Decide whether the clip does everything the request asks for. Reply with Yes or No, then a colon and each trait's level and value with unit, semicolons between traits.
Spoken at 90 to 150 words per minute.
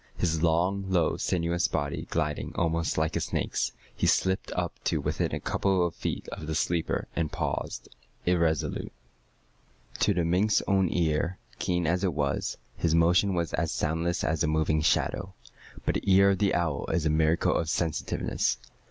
No: average, 170 wpm